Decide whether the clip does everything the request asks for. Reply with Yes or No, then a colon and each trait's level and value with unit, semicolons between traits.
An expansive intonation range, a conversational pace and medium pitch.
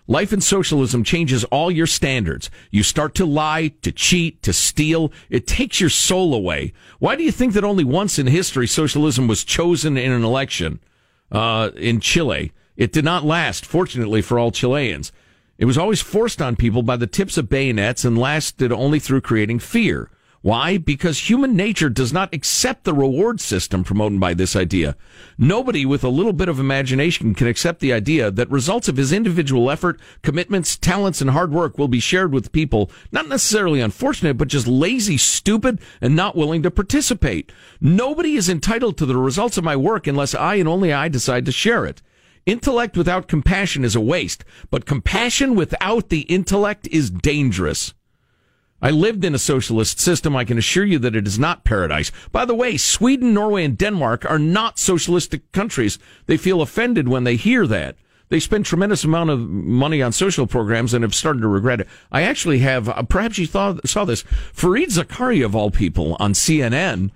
Yes: wide, 7.2 semitones; average, 190 wpm; medium, 150 Hz